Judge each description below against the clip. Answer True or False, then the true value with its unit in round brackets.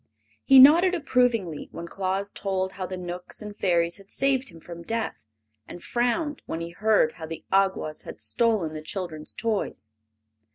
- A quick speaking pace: False (165 wpm)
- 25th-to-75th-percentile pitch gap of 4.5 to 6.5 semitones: True (5.3 semitones)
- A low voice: False (195 Hz)